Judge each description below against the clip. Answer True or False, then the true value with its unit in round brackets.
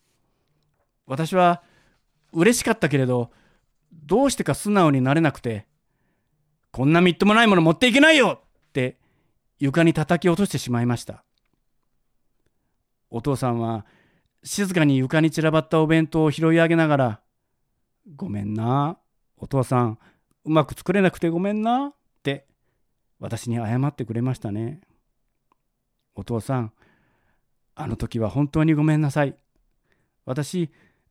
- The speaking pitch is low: False (145 Hz)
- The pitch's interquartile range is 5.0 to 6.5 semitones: True (5.3 semitones)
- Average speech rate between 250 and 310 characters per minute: True (260 characters per minute)